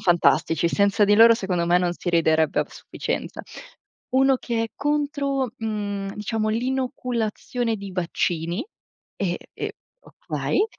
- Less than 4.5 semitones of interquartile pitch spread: No, wide, 5.7 semitones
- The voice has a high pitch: Yes, high, 210 Hz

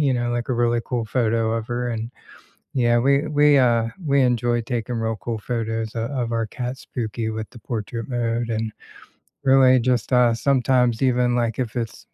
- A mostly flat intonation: Yes, narrow, 1.7 semitones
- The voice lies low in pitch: Yes, low, 120 Hz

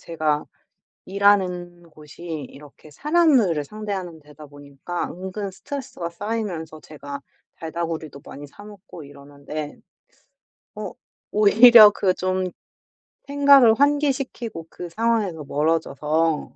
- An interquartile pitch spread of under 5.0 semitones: No, wide, 5.6 semitones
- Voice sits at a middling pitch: Yes, medium, 175 Hz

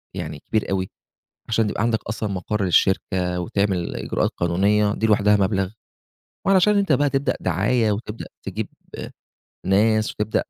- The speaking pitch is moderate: No, low, 105 Hz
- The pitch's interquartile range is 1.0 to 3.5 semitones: Yes, narrow, 2.6 semitones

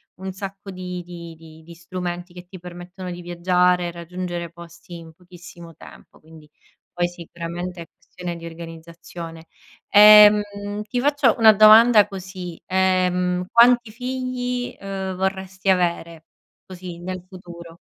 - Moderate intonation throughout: No, narrow, 1.9 semitones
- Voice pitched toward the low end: No, medium, 180 Hz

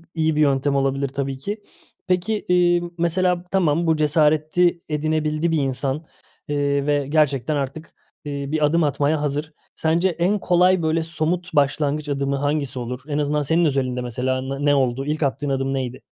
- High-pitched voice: No, medium, 150 Hz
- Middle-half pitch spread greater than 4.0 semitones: No, average, 2.9 semitones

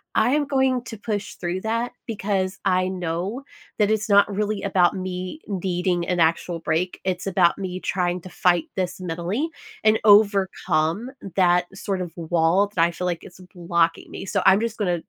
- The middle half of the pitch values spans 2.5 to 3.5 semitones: Yes, average, 2.8 semitones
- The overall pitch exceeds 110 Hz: Yes, medium, 185 Hz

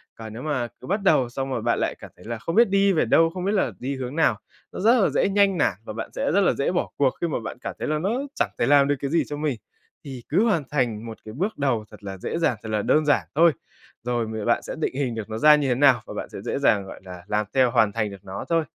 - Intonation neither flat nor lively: No, wide, 6.6 semitones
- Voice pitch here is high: No, low, 135 Hz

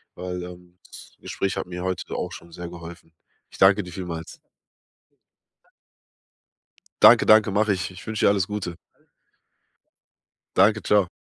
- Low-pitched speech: Yes, very low, 90 Hz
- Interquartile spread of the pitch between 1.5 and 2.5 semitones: Yes, narrow, 2.2 semitones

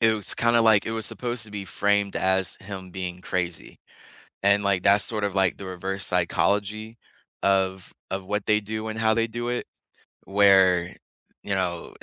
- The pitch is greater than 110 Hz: No, low, 100 Hz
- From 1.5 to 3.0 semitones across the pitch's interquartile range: Yes, narrow, 2.4 semitones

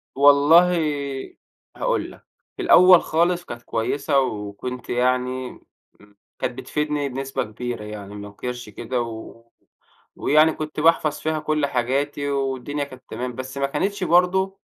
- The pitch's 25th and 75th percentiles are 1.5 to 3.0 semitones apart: No, average, 3.9 semitones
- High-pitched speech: No, low, 135 Hz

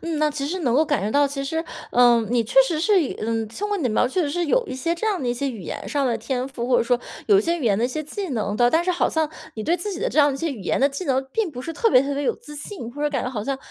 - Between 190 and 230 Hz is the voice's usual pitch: No, very high, 280 Hz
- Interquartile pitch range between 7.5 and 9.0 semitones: No, average, 5.2 semitones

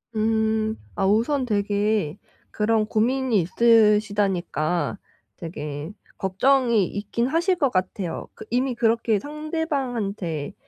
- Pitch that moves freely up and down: No, average, 3.9 semitones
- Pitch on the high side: Yes, high, 220 Hz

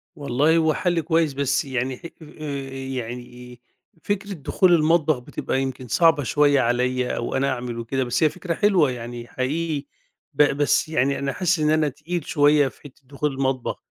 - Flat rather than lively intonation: No, average, 3.7 semitones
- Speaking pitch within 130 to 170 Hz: Yes, medium, 140 Hz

